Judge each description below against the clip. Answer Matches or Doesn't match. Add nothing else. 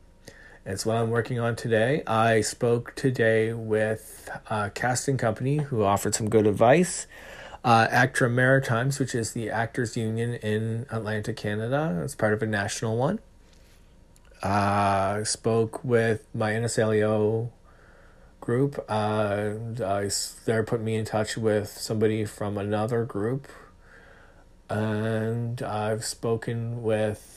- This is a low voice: Matches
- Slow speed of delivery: Matches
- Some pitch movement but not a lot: Doesn't match